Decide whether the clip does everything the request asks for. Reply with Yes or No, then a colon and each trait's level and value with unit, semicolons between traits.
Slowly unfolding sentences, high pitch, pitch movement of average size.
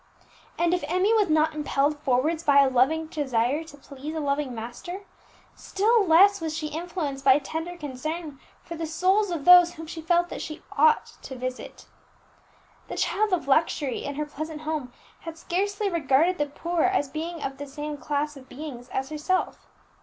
No: average, 180 wpm; very high, 310 Hz; average, 3.6 semitones